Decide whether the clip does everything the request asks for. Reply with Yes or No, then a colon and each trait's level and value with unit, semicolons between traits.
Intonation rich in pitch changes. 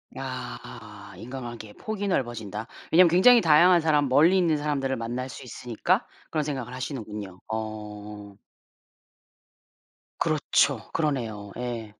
Yes: wide, 5.8 semitones